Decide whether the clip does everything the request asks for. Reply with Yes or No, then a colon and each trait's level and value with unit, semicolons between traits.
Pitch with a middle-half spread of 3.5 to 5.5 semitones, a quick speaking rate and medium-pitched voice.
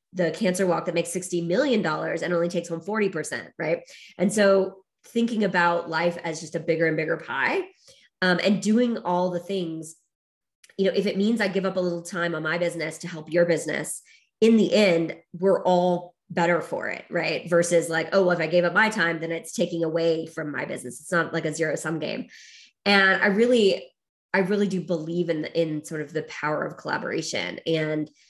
No: average, 2.8 semitones; fast, 210 wpm; medium, 175 Hz